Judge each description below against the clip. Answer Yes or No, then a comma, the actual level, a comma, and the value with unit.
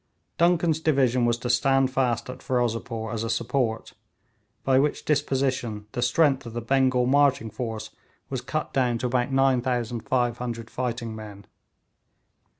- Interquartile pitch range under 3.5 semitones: Yes, narrow, 2.4 semitones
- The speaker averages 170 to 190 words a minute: No, average, 140 wpm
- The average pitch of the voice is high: No, low, 125 Hz